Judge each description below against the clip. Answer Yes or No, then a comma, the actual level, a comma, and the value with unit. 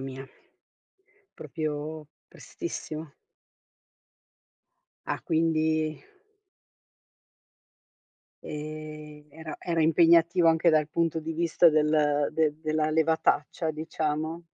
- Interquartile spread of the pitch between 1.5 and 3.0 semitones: No, narrow, 1.1 semitones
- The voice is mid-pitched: Yes, medium, 155 Hz